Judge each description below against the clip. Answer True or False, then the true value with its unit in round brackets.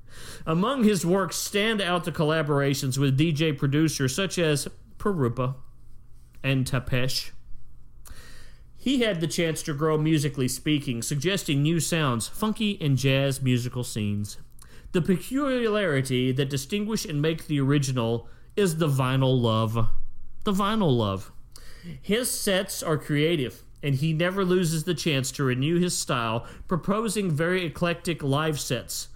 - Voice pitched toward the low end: False (150 Hz)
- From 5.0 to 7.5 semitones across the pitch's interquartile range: True (5.6 semitones)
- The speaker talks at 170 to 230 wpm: False (135 wpm)